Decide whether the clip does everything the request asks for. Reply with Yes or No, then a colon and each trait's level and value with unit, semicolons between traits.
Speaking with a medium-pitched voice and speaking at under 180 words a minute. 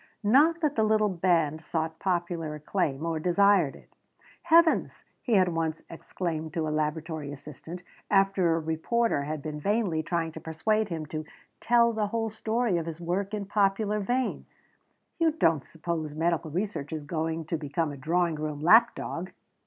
Yes: medium, 170 Hz; average, 170 wpm